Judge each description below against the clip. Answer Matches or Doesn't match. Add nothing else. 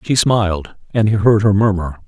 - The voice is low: Matches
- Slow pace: Doesn't match